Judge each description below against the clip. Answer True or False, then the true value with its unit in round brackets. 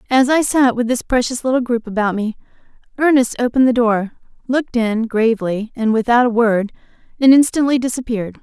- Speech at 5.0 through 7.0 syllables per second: True (5.8 syllables/s)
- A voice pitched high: True (240 Hz)